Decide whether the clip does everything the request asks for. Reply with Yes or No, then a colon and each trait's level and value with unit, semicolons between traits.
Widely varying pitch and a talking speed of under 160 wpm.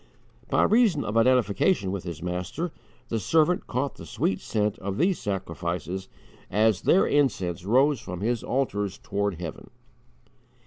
Yes: wide, 6.3 semitones; average, 140 wpm